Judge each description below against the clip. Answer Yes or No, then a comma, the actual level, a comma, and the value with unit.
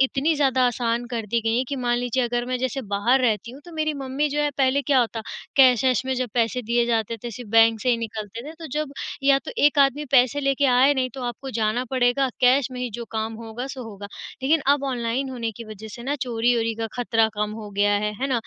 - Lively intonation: No, average, 2.9 semitones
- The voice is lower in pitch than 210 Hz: No, high, 245 Hz